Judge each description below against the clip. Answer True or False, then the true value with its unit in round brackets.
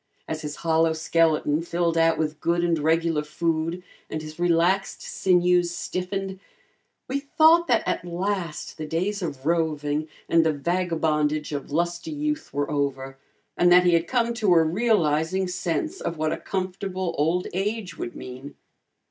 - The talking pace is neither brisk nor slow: True (155 wpm)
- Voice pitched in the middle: True (170 Hz)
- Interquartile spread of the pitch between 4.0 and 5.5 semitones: False (3.0 semitones)